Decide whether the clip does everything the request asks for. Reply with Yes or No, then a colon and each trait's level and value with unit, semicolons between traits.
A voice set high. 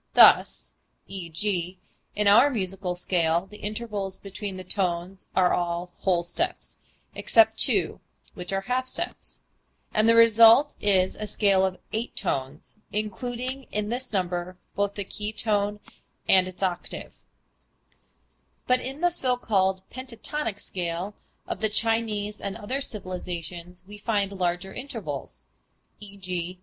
Yes: high, 200 Hz